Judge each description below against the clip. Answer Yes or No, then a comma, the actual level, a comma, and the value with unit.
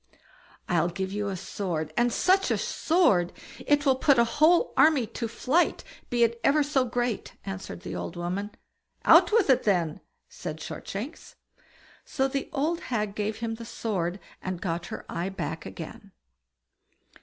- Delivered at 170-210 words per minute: No, average, 160 wpm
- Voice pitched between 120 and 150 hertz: No, high, 225 Hz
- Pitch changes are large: Yes, wide, 6.8 semitones